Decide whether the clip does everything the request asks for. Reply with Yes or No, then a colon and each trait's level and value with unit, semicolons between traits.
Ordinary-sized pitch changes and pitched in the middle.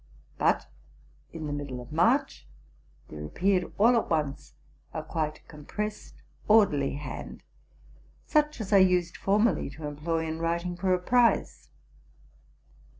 No: wide, 5.7 semitones; medium, 170 Hz